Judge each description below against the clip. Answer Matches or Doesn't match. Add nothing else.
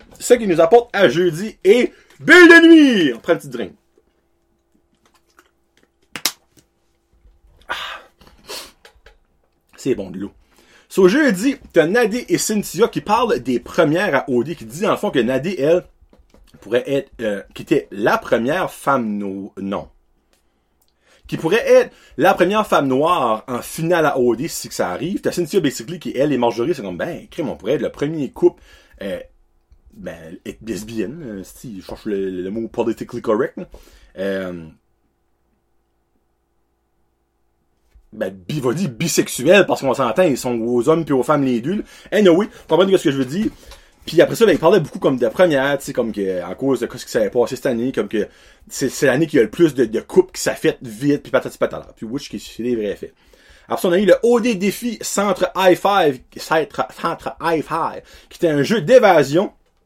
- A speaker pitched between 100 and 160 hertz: Matches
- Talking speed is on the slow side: Doesn't match